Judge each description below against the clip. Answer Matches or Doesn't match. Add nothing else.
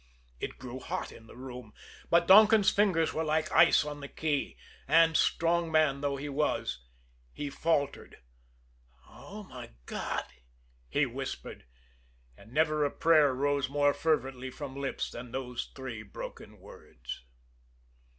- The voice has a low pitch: Doesn't match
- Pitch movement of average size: Matches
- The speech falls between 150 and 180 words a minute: Doesn't match